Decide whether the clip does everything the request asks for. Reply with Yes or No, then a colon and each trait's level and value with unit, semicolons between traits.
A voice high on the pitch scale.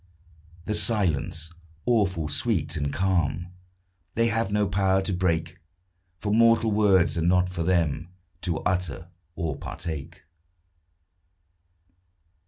No: very low, 90 Hz